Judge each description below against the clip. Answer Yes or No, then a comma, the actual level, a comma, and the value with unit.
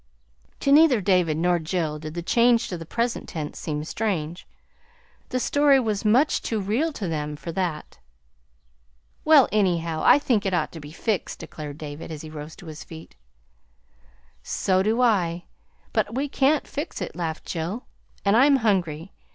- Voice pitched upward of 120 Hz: Yes, medium, 185 Hz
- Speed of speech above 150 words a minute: Yes, average, 170 wpm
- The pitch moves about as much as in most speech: No, wide, 6.6 semitones